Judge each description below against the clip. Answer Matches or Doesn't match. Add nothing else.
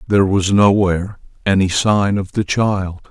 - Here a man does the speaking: Matches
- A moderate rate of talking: Matches